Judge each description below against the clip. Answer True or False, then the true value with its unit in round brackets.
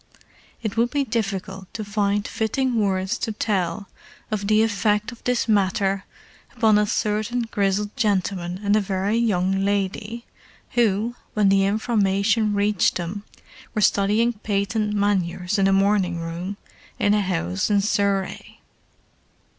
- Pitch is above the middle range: True (205 Hz)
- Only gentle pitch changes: True (1.9 semitones)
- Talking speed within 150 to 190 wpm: False (140 wpm)